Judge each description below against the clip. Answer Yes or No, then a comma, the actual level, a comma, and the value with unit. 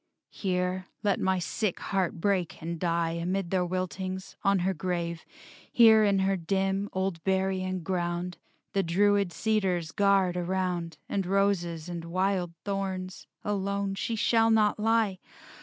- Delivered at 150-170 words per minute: No, average, 140 wpm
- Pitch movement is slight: Yes, narrow, 2.1 semitones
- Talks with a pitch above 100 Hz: Yes, high, 190 Hz